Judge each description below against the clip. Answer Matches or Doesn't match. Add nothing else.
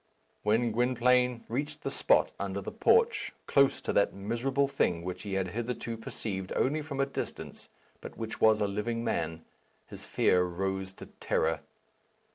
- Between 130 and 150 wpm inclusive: Doesn't match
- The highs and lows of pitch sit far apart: Doesn't match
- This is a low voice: Matches